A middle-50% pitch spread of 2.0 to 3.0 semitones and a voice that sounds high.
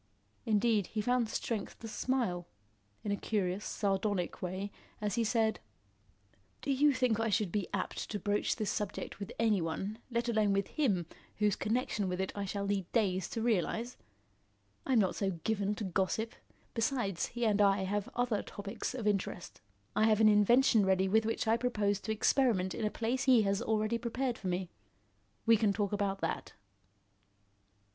Yes: narrow, 2.6 semitones; high, 210 Hz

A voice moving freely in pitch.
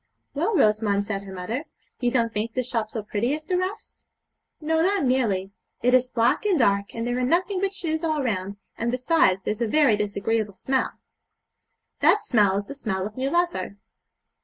Yes: wide, 6.7 semitones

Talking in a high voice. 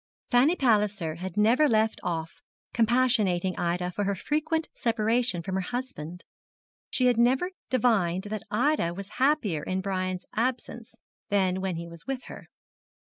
Yes: high, 210 Hz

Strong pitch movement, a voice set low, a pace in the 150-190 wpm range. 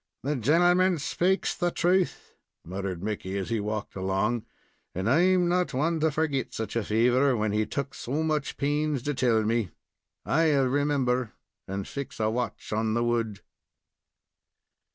Yes: wide, 5.9 semitones; low, 125 Hz; average, 155 wpm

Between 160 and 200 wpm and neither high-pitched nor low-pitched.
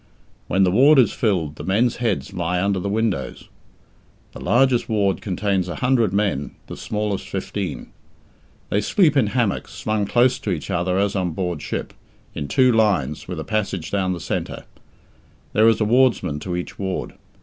No: average, 175 wpm; low, 100 Hz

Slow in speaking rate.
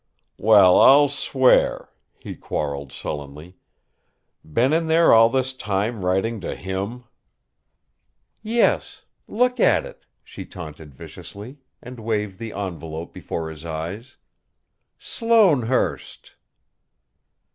Yes: slow, 105 wpm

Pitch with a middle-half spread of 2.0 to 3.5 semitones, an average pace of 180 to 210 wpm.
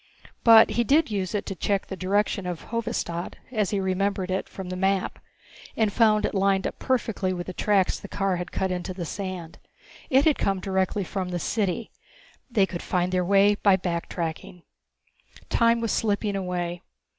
Yes: narrow, 2.5 semitones; average, 185 wpm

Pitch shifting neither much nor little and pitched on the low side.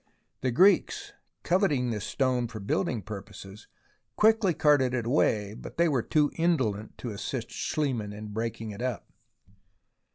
No: wide, 5.8 semitones; low, 120 Hz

